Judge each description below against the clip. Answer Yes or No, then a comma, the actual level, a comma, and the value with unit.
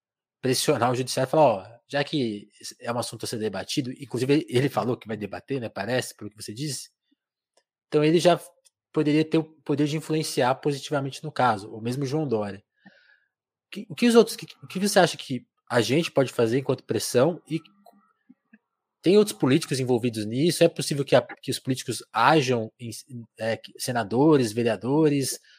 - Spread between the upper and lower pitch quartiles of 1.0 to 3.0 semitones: No, average, 4.7 semitones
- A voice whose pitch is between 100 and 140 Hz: Yes, low, 135 Hz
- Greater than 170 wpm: Yes, average, 180 wpm